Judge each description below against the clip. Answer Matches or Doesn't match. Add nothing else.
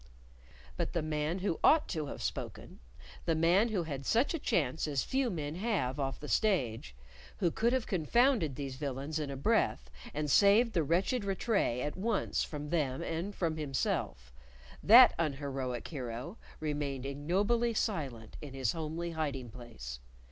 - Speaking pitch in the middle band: Matches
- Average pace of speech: Matches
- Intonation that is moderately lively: Doesn't match